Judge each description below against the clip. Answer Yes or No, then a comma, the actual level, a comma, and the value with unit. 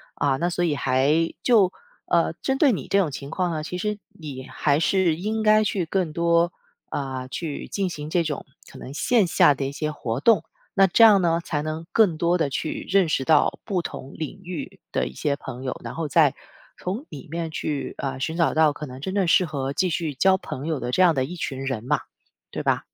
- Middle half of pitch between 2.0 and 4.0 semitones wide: No, average, 4.6 semitones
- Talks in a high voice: No, medium, 160 Hz